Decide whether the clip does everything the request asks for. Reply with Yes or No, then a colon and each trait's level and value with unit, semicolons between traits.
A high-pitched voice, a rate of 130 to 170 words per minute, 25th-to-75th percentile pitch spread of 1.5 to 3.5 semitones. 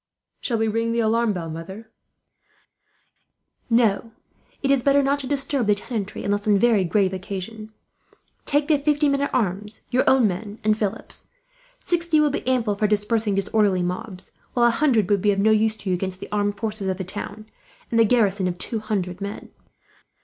No: high, 215 Hz; average, 190 wpm; average, 3.2 semitones